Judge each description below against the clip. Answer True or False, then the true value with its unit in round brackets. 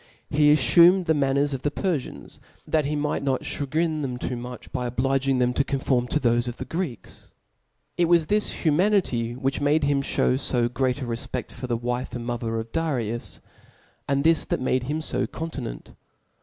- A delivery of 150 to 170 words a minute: False (195 wpm)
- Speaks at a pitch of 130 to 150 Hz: True (135 Hz)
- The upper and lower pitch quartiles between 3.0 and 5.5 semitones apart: True (3.7 semitones)